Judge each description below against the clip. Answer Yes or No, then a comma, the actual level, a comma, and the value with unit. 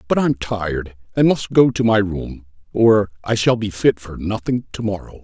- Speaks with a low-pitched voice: Yes, low, 105 Hz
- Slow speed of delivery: No, fast, 205 wpm